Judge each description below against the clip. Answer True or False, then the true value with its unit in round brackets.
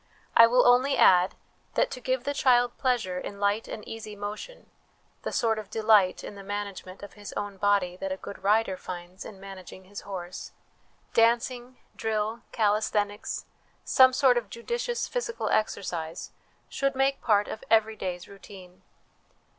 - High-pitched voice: True (210 Hz)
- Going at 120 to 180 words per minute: True (160 wpm)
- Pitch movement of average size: True (3.8 semitones)